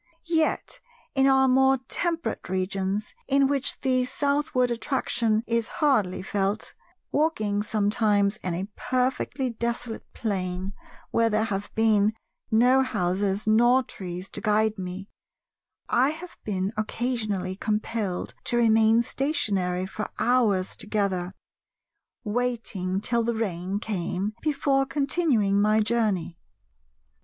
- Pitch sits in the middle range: No, high, 220 Hz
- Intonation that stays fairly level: No, average, 4.3 semitones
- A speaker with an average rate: No, slow, 115 wpm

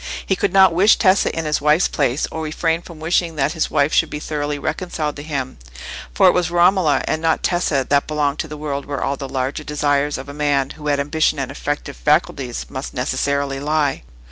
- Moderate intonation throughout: No, narrow, 2.2 semitones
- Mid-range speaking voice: Yes, medium, 150 Hz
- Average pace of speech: No, fast, 215 wpm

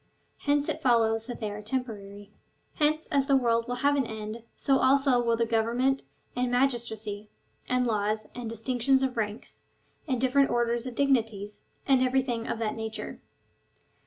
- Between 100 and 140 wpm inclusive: No, average, 160 wpm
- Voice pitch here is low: No, high, 240 Hz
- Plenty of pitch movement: No, average, 3.1 semitones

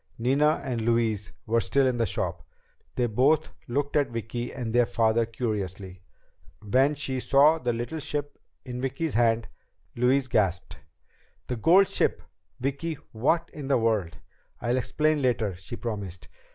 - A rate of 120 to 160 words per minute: Yes, average, 150 wpm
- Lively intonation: No, average, 3.8 semitones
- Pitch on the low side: Yes, low, 120 Hz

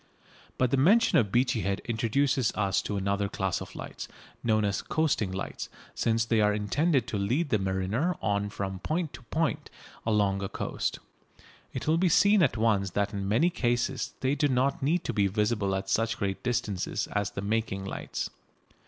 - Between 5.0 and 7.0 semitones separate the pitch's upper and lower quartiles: Yes, average, 5.3 semitones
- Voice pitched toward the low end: Yes, low, 110 Hz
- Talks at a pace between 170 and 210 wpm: Yes, average, 185 wpm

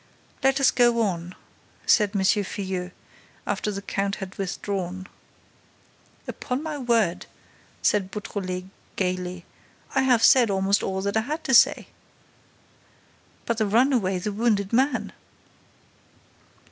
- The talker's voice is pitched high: Yes, high, 200 Hz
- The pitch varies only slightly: No, average, 4.0 semitones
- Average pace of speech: No, slow, 120 wpm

